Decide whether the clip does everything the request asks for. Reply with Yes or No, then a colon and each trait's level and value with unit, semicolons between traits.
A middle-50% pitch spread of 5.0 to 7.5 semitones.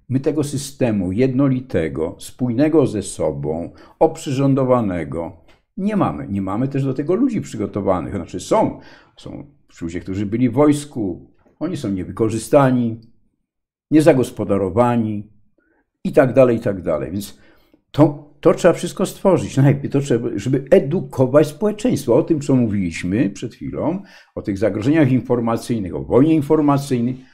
Yes: average, 5.3 semitones